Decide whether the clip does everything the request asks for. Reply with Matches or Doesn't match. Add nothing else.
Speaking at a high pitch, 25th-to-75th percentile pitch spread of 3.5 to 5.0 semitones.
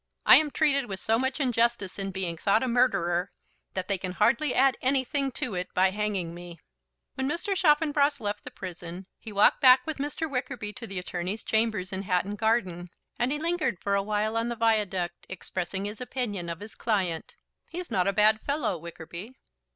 Doesn't match